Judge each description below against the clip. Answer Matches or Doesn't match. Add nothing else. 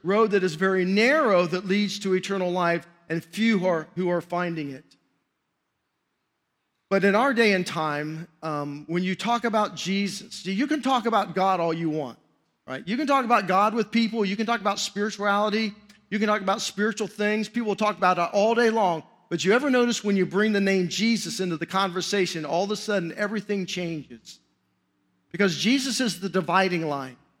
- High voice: Matches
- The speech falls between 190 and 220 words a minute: Matches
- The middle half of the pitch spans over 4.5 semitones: Doesn't match